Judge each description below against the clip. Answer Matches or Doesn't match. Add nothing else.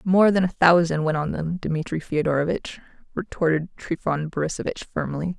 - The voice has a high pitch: Doesn't match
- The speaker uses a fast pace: Doesn't match